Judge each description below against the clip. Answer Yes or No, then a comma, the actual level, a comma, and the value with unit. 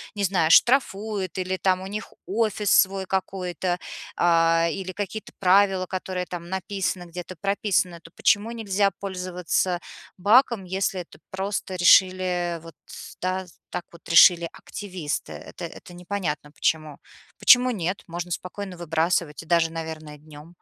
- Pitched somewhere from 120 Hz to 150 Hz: No, medium, 185 Hz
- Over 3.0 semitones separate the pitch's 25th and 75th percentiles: No, narrow, 2.4 semitones